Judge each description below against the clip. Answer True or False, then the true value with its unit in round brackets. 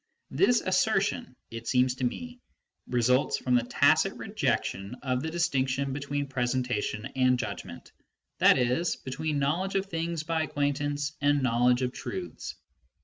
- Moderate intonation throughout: True (4.2 semitones)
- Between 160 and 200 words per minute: False (140 wpm)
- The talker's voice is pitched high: False (135 Hz)